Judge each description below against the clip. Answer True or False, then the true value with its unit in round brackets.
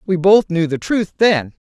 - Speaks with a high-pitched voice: False (180 Hz)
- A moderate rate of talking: False (215 wpm)